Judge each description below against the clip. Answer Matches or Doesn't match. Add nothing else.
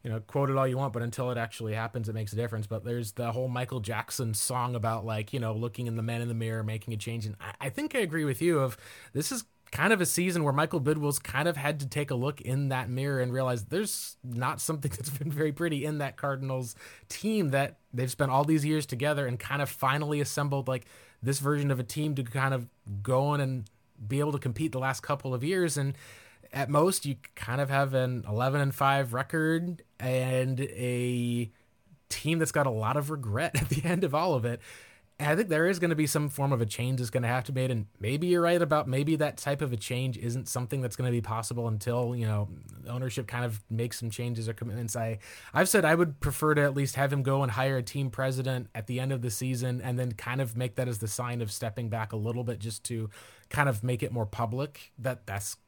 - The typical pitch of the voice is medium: Doesn't match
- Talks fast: Matches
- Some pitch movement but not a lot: Matches